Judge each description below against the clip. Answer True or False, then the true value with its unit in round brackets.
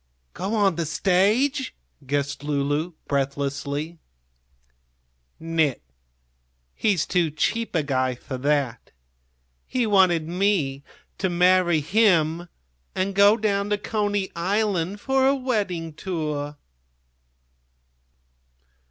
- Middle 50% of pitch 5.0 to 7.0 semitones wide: True (5.6 semitones)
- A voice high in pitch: False (175 Hz)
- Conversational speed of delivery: False (100 wpm)